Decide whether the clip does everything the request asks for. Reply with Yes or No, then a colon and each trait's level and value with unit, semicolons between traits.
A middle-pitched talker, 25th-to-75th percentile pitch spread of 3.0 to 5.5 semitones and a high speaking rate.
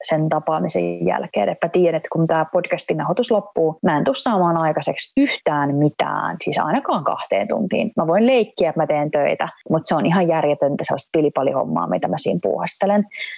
Yes: medium, 160 Hz; average, 3.8 semitones; fast, 185 wpm